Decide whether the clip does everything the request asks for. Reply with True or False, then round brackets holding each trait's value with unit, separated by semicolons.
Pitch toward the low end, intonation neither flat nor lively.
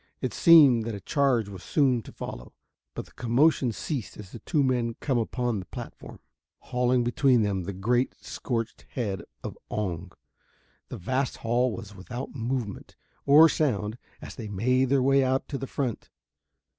True (120 Hz; 3.8 semitones)